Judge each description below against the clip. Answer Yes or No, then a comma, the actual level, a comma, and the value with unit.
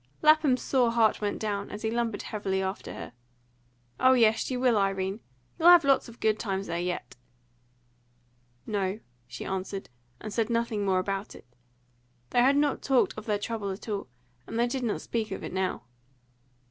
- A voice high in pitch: Yes, high, 215 Hz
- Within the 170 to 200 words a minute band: Yes, average, 180 wpm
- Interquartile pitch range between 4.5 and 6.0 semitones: No, average, 3.5 semitones